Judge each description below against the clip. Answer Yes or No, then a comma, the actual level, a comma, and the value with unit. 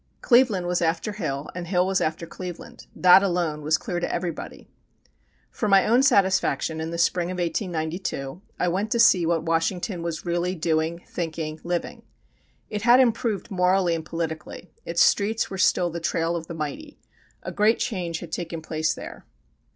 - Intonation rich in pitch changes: No, average, 2.8 semitones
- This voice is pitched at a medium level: Yes, medium, 175 Hz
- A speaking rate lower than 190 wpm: Yes, average, 175 wpm